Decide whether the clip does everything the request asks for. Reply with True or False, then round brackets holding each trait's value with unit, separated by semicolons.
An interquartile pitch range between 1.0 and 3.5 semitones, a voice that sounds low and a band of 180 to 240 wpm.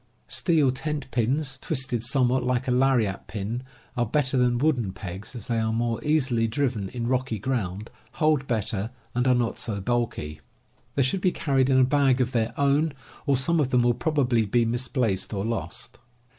True (3.0 semitones; 125 Hz; 185 wpm)